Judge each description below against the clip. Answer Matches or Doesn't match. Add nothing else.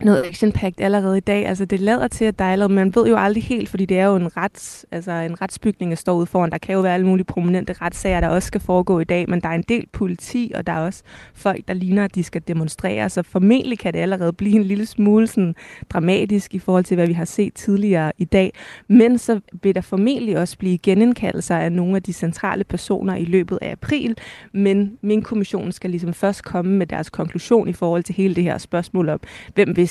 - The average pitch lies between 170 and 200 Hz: Matches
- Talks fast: Matches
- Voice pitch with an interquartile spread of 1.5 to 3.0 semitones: Matches